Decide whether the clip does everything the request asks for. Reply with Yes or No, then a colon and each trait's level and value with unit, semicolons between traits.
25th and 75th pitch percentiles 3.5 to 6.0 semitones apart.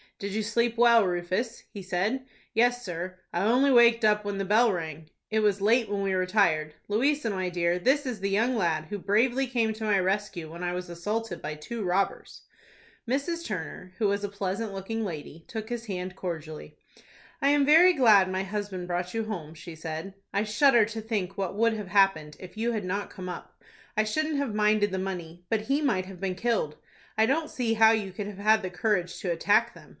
Yes: average, 3.8 semitones